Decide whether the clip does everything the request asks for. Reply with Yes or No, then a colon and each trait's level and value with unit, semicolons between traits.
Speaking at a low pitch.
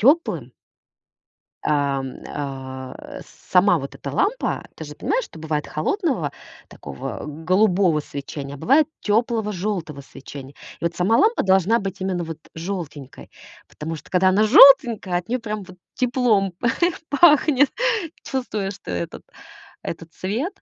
No: medium, 185 Hz